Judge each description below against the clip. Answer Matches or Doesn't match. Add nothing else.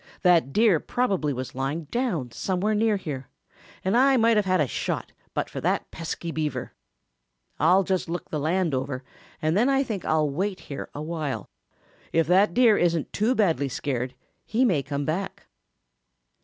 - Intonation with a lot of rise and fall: Matches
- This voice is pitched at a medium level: Matches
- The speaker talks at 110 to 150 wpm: Doesn't match